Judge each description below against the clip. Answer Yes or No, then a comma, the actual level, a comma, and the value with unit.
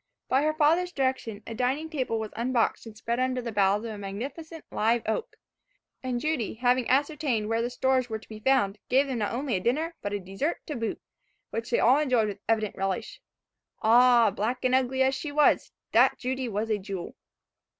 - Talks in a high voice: Yes, high, 245 Hz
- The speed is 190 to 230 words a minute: Yes, average, 200 wpm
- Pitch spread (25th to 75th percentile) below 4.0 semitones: Yes, average, 3.4 semitones